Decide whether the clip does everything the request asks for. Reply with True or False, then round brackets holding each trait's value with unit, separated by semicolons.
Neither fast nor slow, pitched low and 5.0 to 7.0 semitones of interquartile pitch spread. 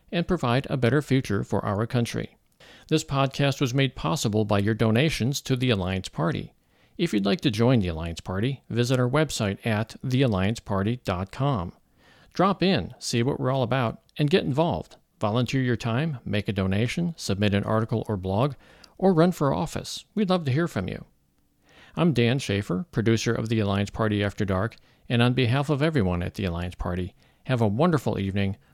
True (180 wpm; 115 Hz; 5.5 semitones)